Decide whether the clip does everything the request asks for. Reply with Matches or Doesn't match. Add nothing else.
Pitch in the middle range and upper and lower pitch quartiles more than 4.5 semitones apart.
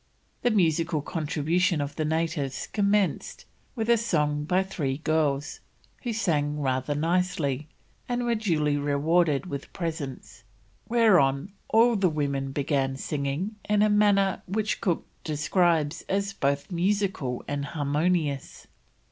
Matches